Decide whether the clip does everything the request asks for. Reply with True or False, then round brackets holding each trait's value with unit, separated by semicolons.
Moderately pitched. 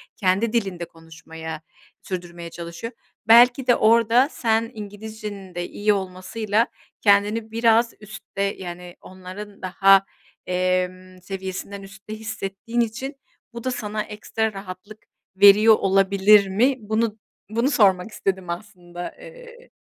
False (200 Hz)